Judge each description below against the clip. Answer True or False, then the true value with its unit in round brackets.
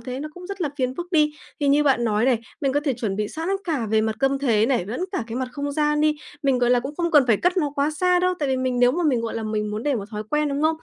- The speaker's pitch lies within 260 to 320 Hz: True (270 Hz)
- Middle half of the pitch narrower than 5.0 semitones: True (4.4 semitones)